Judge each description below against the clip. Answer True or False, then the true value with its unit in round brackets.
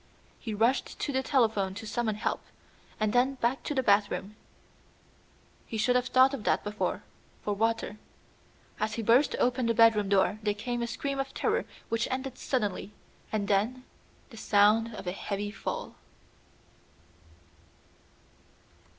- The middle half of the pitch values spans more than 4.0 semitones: False (3.3 semitones)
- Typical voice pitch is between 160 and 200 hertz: False (225 Hz)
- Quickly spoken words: False (150 wpm)